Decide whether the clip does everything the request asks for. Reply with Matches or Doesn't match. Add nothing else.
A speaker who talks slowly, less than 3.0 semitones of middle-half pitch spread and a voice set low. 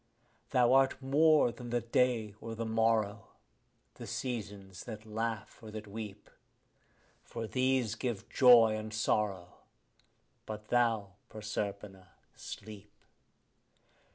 Matches